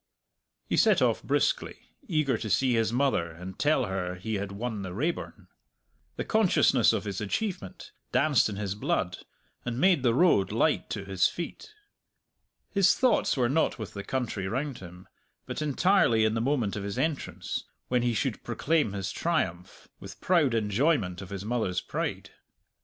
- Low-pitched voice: Yes, low, 115 Hz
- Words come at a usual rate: Yes, average, 170 wpm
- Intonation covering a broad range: Yes, wide, 7.0 semitones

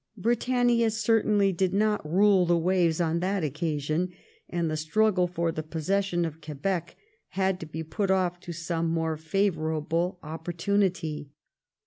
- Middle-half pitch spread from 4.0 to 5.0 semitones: No, average, 3.4 semitones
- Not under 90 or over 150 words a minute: Yes, average, 140 wpm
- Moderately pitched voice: Yes, medium, 175 Hz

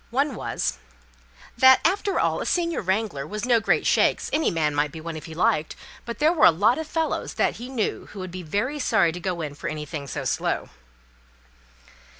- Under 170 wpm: No, fast, 205 wpm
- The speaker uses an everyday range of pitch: No, wide, 8.6 semitones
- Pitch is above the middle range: Yes, high, 205 Hz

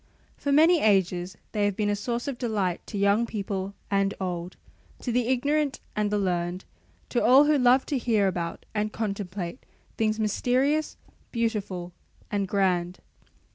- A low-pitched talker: No, high, 210 Hz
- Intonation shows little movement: No, average, 4.3 semitones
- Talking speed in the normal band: Yes, average, 155 wpm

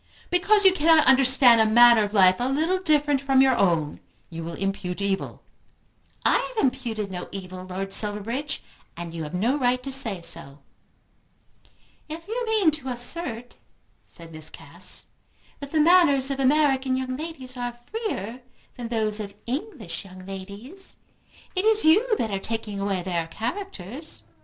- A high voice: Yes, high, 245 Hz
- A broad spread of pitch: Yes, wide, 7.2 semitones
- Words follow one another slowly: No, average, 160 wpm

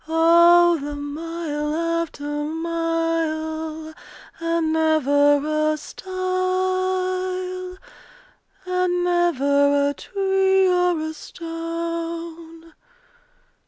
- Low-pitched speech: No, very high, 330 Hz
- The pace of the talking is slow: Yes, slow, 70 wpm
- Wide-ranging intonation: No, narrow, 2.4 semitones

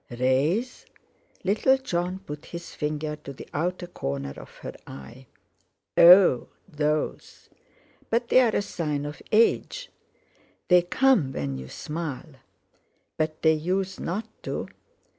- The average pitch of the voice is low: No, medium, 160 Hz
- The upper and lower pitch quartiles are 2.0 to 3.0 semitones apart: No, average, 4.8 semitones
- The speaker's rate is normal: No, slow, 120 wpm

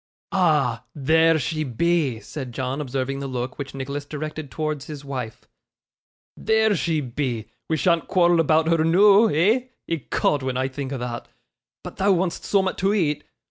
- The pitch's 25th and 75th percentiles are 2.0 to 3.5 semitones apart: No, average, 4.3 semitones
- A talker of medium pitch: Yes, medium, 150 Hz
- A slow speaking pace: No, average, 165 wpm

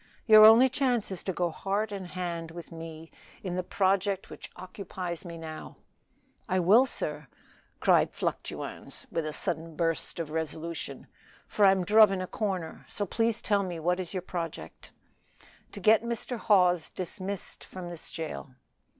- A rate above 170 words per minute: No, average, 160 wpm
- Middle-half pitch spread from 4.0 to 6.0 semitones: No, average, 3.4 semitones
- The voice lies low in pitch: No, medium, 185 Hz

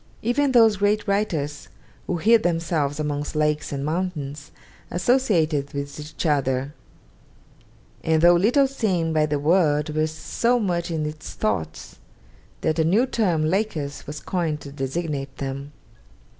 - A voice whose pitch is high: No, medium, 155 Hz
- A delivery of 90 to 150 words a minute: Yes, average, 140 wpm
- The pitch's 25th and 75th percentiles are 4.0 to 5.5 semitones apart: Yes, average, 4.4 semitones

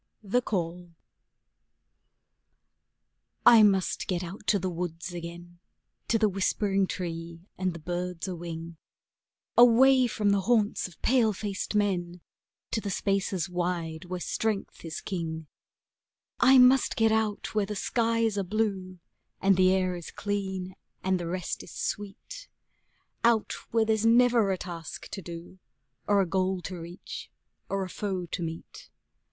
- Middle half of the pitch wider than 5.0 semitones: No, average, 3.4 semitones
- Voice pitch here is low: No, high, 190 Hz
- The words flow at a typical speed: Yes, average, 145 wpm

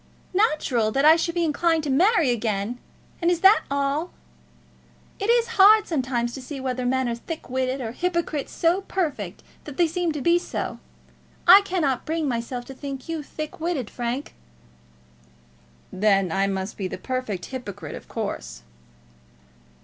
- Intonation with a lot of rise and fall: Yes, wide, 6.0 semitones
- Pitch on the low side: No, very high, 275 Hz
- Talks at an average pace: Yes, average, 160 wpm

